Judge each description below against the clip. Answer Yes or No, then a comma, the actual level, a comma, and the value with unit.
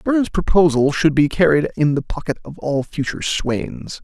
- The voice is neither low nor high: Yes, medium, 155 Hz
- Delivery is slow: No, average, 180 wpm